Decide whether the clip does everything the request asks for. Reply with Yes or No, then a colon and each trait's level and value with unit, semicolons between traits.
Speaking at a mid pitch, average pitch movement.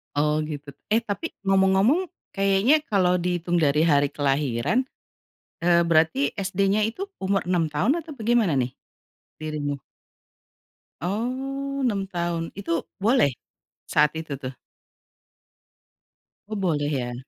No: medium, 180 Hz; wide, 6.1 semitones